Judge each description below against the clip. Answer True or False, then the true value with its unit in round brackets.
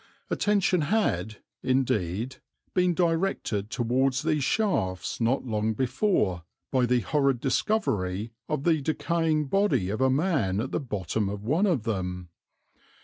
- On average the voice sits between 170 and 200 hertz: False (130 Hz)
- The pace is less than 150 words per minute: True (135 wpm)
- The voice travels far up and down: True (7.4 semitones)